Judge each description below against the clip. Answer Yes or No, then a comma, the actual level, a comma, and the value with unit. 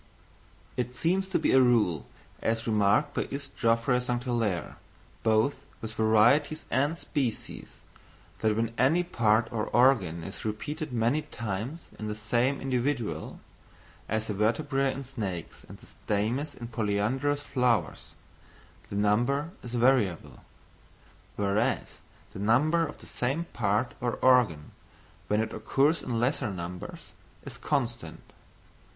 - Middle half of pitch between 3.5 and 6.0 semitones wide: Yes, average, 4.1 semitones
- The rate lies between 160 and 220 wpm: No, slow, 135 wpm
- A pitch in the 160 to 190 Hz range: No, low, 120 Hz